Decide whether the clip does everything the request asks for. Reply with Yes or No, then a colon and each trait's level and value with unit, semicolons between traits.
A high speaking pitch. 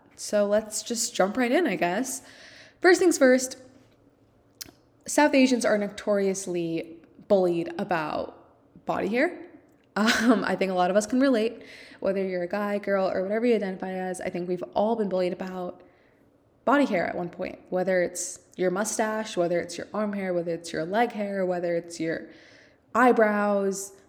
Yes: high, 205 Hz